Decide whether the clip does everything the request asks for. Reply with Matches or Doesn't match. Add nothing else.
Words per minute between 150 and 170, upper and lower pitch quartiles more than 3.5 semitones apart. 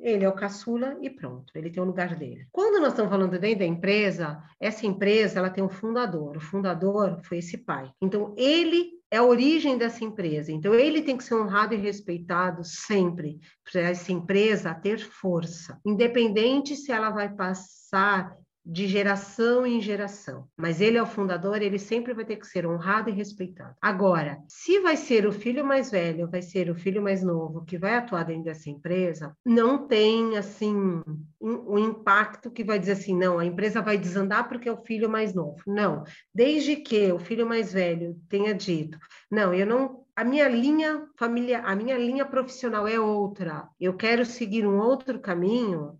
Doesn't match